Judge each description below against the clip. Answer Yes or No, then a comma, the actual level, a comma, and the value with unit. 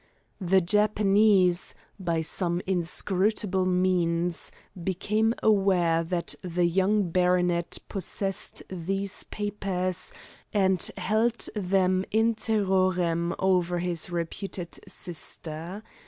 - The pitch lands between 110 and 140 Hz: No, medium, 185 Hz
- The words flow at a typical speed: No, slow, 90 wpm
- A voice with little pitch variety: Yes, narrow, 2.3 semitones